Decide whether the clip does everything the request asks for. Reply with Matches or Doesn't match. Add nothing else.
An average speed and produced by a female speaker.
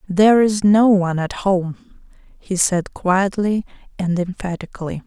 Doesn't match